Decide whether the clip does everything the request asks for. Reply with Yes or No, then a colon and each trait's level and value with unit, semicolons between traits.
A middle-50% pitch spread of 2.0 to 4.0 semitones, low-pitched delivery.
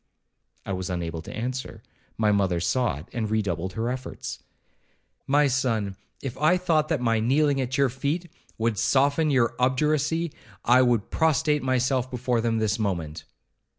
No: average, 4.7 semitones; low, 125 Hz